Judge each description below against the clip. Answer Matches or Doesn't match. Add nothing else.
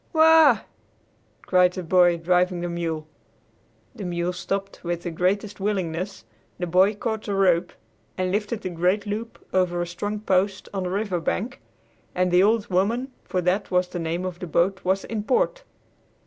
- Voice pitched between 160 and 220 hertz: Matches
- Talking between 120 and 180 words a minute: Matches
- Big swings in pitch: Doesn't match